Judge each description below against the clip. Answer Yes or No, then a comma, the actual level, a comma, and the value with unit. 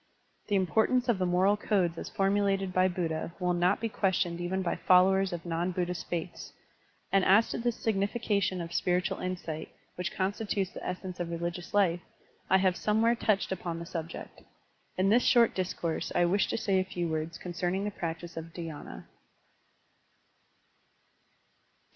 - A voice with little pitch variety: Yes, narrow, 2.3 semitones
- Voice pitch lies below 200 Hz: Yes, medium, 185 Hz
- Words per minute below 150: No, average, 160 wpm